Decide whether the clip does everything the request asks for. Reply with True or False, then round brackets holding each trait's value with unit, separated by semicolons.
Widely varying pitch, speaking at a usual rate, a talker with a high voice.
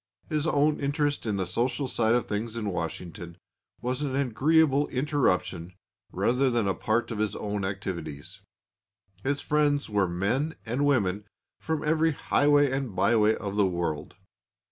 False (6.6 semitones; 150 wpm; 120 Hz)